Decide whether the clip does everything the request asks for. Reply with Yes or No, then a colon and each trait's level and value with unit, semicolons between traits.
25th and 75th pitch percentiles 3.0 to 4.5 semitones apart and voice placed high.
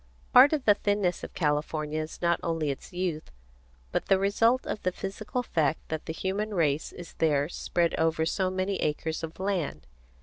No: average, 4.0 semitones; medium, 175 Hz